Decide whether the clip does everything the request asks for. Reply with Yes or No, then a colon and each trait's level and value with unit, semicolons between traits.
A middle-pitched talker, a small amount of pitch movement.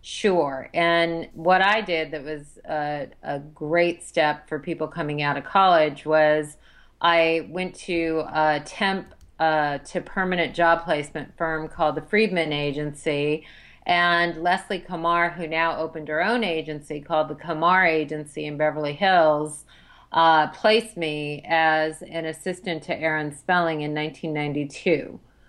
Yes: medium, 160 Hz; narrow, 2.2 semitones